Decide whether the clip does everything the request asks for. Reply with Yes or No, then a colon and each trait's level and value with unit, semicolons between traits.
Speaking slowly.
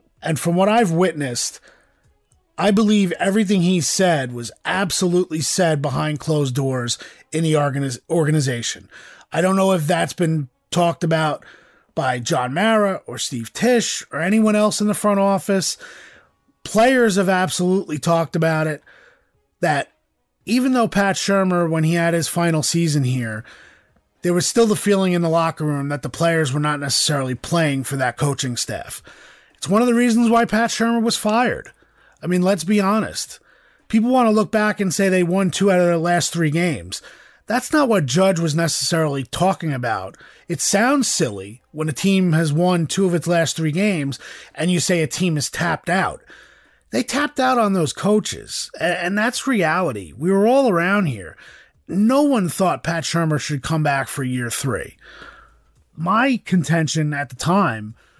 No: average, 175 wpm